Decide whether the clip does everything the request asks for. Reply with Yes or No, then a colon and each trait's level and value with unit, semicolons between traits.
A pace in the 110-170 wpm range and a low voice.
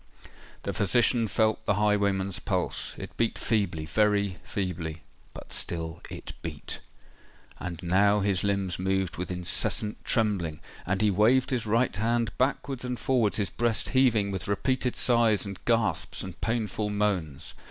Yes: slow, 135 wpm; low, 100 Hz